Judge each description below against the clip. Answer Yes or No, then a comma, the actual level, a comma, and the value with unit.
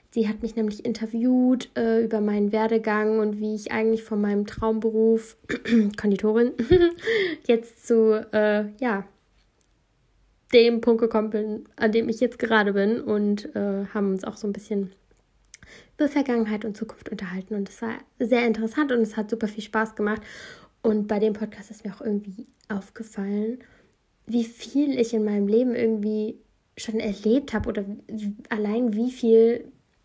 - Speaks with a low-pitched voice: No, high, 220 Hz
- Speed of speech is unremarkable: Yes, average, 160 wpm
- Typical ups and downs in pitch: No, narrow, 1.7 semitones